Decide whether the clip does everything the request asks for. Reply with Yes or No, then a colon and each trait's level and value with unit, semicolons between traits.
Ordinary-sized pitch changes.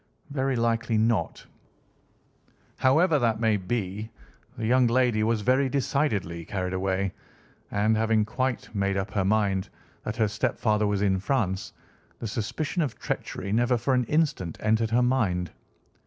Yes: average, 4.0 semitones